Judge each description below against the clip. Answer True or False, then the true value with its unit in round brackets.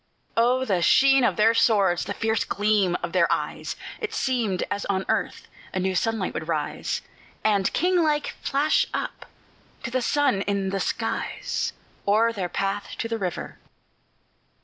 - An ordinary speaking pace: True (160 wpm)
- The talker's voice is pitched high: True (215 Hz)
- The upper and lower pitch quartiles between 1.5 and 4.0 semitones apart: False (4.8 semitones)